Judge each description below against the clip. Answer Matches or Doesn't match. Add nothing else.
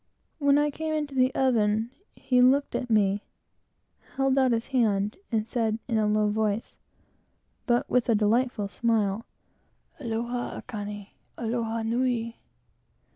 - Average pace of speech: Doesn't match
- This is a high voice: Matches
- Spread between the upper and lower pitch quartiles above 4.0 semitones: Doesn't match